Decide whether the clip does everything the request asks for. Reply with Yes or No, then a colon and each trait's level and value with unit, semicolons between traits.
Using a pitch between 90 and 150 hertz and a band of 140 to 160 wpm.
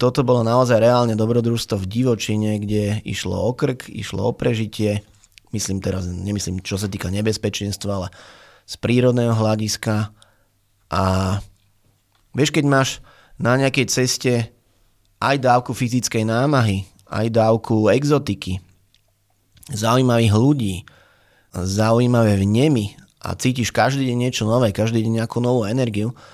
No: low, 110 Hz; average, 125 wpm